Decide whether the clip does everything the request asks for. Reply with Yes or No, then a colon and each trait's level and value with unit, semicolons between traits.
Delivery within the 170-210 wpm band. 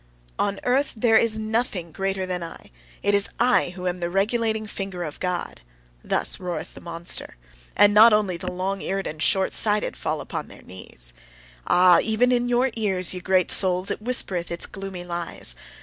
Yes: average, 180 wpm